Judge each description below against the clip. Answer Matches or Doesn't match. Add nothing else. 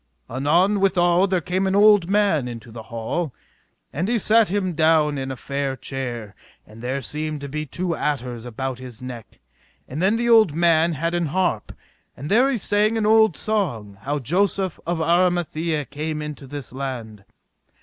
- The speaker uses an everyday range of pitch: Doesn't match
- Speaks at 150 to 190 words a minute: Matches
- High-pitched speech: Doesn't match